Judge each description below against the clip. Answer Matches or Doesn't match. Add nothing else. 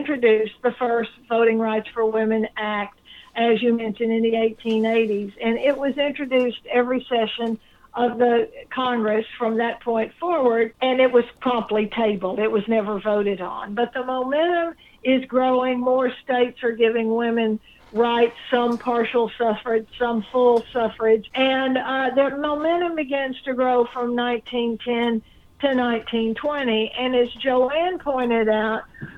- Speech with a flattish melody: Matches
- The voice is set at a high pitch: Matches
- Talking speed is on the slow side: Doesn't match